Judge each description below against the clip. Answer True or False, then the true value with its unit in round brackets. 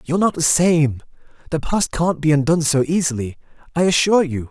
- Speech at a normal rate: True (185 wpm)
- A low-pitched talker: False (155 Hz)